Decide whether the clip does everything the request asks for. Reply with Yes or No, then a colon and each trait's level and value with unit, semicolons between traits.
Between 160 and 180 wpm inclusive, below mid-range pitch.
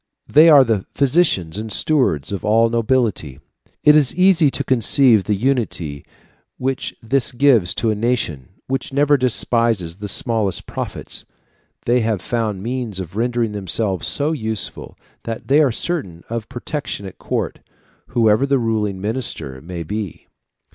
No: average, 150 wpm; low, 115 Hz